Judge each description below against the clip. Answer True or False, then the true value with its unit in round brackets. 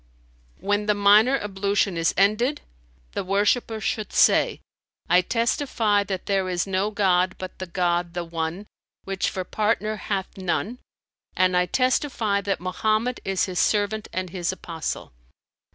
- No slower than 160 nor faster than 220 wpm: False (145 wpm)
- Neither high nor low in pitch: False (195 Hz)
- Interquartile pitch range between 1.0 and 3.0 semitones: True (2.7 semitones)